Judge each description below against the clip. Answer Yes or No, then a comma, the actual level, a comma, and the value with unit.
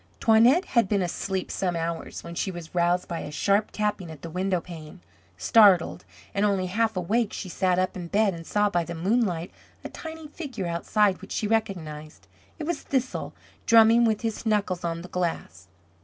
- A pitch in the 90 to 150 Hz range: No, high, 190 Hz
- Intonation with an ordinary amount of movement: Yes, average, 4.3 semitones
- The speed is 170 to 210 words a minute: Yes, average, 185 wpm